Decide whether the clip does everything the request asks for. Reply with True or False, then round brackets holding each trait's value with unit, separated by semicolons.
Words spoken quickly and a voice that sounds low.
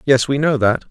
True (265 wpm; 130 Hz)